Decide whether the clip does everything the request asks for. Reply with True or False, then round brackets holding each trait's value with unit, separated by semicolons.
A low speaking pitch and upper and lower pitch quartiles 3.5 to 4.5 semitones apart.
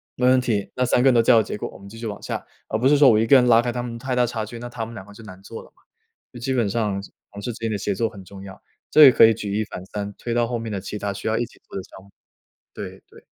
False (115 Hz; 3.0 semitones)